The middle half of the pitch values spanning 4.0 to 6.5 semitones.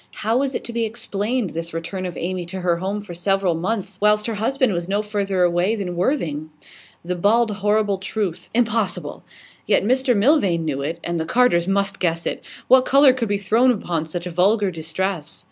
Yes: average, 4.3 semitones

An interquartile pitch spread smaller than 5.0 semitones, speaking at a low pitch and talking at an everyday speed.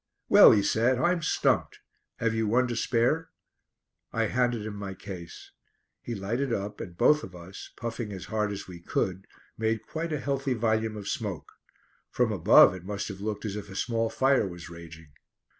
Yes: average, 3.6 semitones; low, 110 Hz; average, 185 wpm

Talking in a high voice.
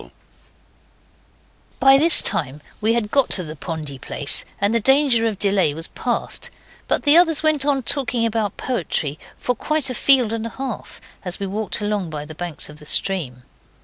Yes: high, 215 Hz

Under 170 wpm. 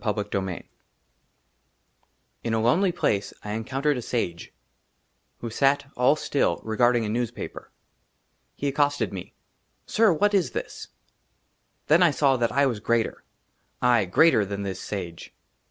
Yes: average, 145 wpm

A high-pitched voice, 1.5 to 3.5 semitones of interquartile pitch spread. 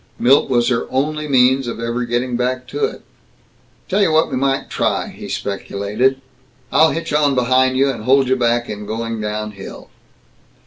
No: low, 125 Hz; average, 2.8 semitones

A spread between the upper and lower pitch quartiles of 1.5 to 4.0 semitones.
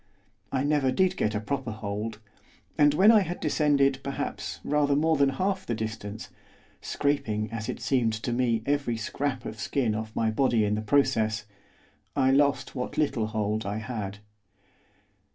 No: average, 4.7 semitones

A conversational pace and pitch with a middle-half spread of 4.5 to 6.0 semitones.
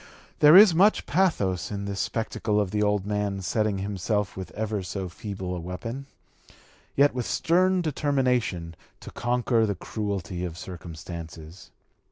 Yes: average, 145 wpm; average, 5.3 semitones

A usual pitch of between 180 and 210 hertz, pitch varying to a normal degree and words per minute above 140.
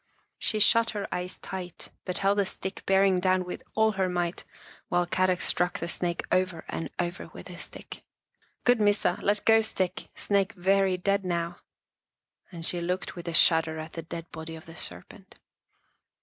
No: medium, 185 Hz; narrow, 2.3 semitones; average, 180 wpm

